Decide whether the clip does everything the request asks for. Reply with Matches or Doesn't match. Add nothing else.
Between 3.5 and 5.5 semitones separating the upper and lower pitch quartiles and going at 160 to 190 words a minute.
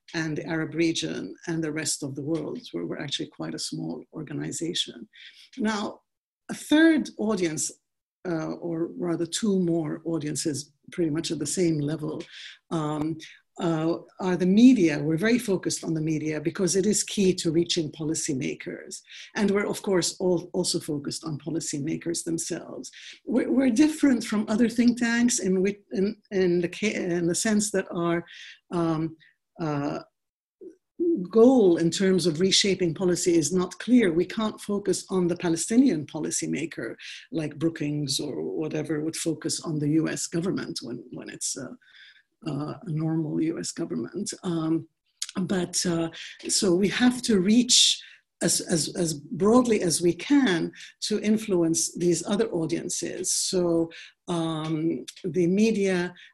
Doesn't match